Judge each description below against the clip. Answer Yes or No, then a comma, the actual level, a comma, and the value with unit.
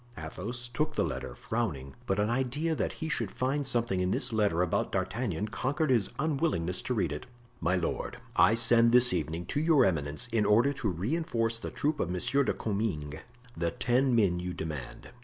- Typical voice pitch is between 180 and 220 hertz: No, low, 115 Hz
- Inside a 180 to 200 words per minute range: Yes, average, 195 wpm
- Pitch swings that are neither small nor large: No, wide, 6.6 semitones